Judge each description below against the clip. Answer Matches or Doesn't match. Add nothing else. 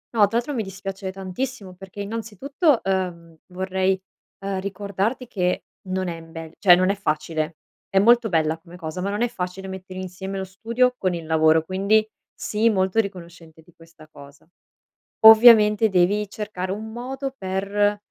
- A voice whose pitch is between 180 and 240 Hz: Matches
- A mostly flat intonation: Doesn't match